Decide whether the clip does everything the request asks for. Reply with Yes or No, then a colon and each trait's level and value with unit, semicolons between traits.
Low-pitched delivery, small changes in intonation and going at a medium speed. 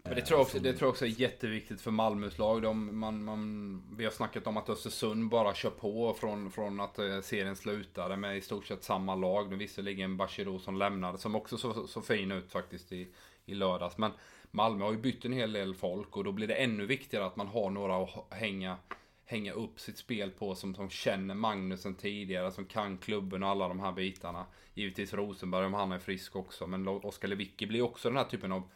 No: low, 100 Hz; narrow, 2.3 semitones; fast, 220 wpm